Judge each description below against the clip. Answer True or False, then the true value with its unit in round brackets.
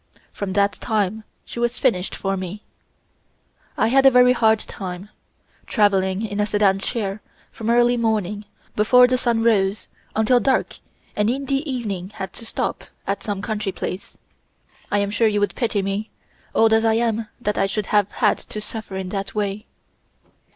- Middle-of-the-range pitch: False (210 Hz)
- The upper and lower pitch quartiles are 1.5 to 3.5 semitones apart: True (2.7 semitones)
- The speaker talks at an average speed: True (175 wpm)